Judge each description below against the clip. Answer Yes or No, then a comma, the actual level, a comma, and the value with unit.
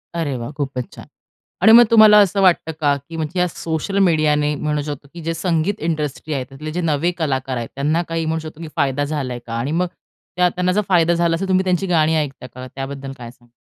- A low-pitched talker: No, medium, 155 Hz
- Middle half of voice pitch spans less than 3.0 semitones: No, average, 3.7 semitones